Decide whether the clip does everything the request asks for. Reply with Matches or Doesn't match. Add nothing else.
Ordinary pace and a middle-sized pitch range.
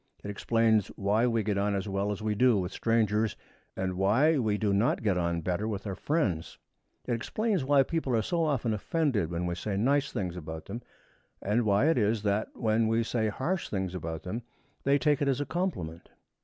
Doesn't match